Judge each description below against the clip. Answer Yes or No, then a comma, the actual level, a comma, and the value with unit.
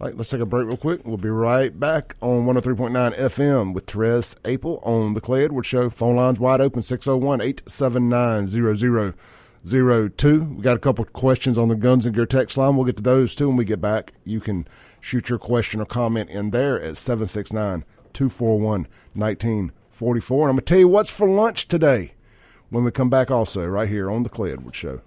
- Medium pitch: No, low, 120 Hz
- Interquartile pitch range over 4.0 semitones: No, average, 3.0 semitones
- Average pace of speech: Yes, average, 195 wpm